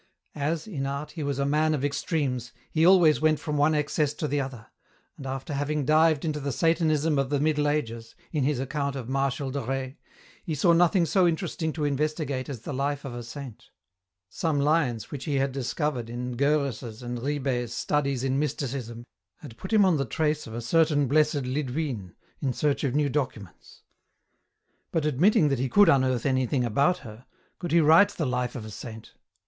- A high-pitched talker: No, medium, 140 Hz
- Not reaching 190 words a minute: No, average, 200 wpm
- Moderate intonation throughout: Yes, average, 3.0 semitones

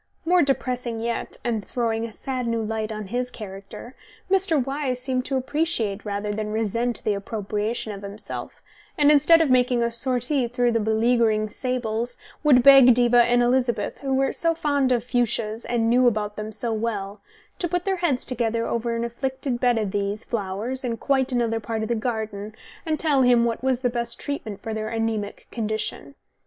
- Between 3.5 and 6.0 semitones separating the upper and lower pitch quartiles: No, average, 2.9 semitones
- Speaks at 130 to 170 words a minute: No, average, 185 wpm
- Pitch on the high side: Yes, high, 235 Hz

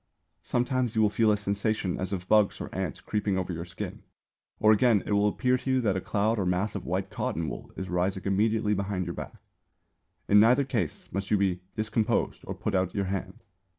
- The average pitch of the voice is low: Yes, low, 100 Hz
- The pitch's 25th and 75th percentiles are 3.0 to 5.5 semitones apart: No, narrow, 2.6 semitones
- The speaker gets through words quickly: Yes, fast, 215 wpm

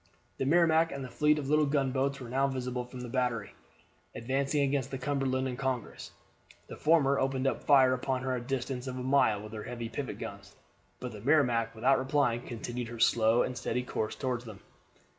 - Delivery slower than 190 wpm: No, average, 200 wpm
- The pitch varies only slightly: Yes, narrow, 2.2 semitones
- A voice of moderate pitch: No, low, 130 Hz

